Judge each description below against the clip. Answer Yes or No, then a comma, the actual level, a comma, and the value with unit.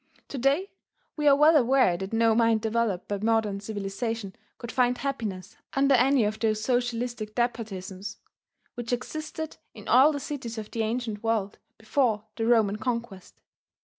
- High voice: Yes, high, 230 Hz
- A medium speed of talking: Yes, average, 155 wpm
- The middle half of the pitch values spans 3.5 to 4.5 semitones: No, average, 3.0 semitones